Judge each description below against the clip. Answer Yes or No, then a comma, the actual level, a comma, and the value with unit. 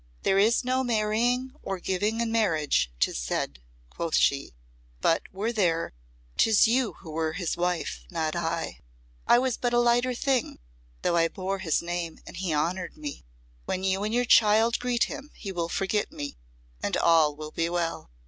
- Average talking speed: Yes, average, 175 wpm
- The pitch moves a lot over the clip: Yes, wide, 5.8 semitones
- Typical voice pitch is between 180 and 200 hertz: Yes, high, 190 Hz